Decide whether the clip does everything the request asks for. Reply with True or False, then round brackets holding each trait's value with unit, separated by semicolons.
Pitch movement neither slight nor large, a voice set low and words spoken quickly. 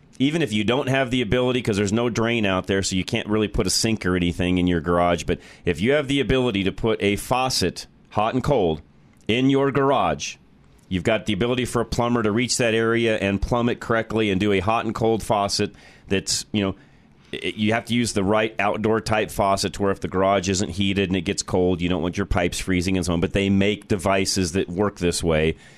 True (3.3 semitones; 105 Hz; 240 wpm)